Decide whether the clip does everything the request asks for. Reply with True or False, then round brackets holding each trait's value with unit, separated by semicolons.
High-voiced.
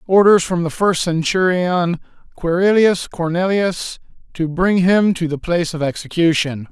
False (175 Hz)